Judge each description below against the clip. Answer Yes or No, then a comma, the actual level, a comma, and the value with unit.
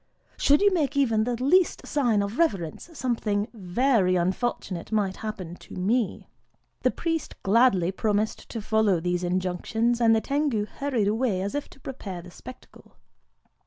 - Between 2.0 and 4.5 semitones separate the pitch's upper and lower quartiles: No, average, 5.3 semitones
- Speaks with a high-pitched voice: Yes, high, 220 Hz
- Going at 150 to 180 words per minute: Yes, average, 155 wpm